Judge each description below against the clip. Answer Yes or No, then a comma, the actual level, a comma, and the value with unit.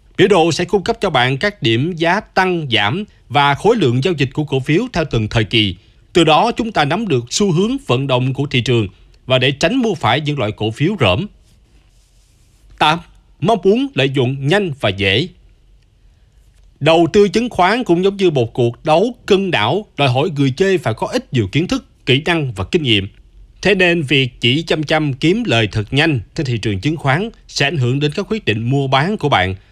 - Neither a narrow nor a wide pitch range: No, wide, 7.4 semitones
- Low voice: No, medium, 145 Hz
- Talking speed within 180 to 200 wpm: No, average, 220 wpm